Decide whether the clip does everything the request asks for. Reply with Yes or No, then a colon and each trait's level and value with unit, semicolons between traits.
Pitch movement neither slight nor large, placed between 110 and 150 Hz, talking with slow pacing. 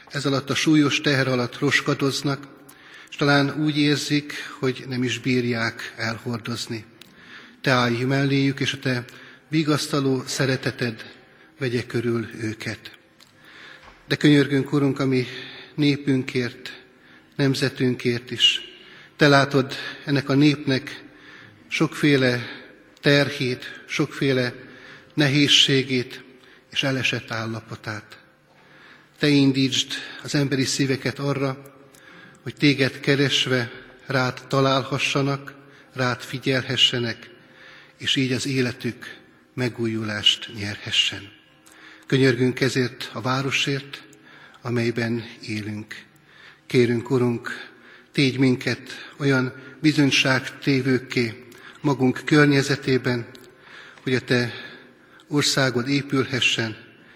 No: narrow, 2.2 semitones; low, 130 Hz; slow, 90 wpm